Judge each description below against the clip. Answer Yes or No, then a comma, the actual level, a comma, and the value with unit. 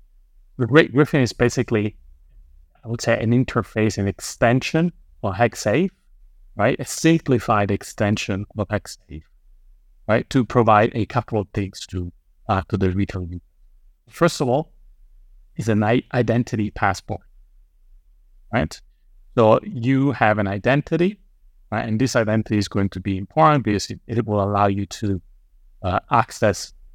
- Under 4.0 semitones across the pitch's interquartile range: No, average, 5.1 semitones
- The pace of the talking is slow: Yes, slow, 145 wpm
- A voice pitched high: No, low, 105 Hz